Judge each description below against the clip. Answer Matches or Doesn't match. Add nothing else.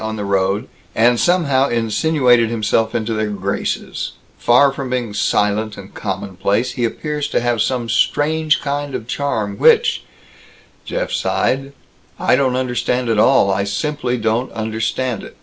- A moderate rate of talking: Matches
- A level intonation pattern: Doesn't match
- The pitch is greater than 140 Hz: Doesn't match